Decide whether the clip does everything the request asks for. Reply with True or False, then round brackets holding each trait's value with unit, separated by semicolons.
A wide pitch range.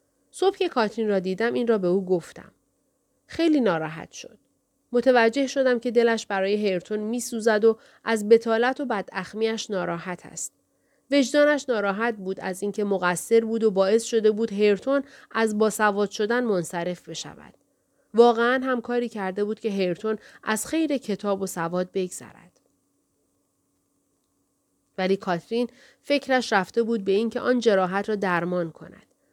False (4.0 semitones)